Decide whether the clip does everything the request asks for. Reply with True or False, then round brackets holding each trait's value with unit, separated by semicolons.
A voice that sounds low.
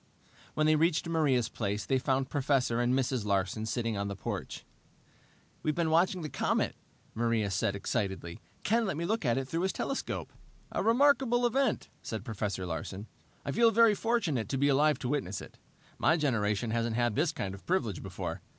True (130 Hz)